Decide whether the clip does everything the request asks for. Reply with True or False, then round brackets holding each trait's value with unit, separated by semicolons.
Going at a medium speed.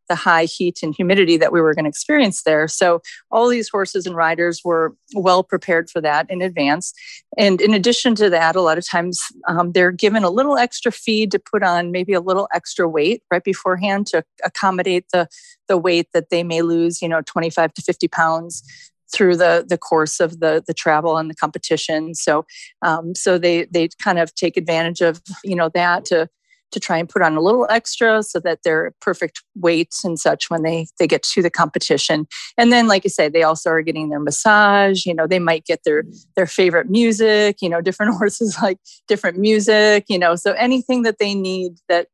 False (210 wpm)